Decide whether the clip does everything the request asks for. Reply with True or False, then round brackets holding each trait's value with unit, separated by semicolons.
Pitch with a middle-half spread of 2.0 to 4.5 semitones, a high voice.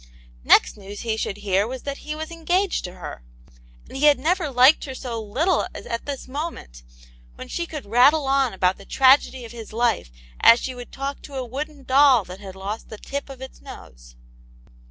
False (5.1 semitones; 260 Hz)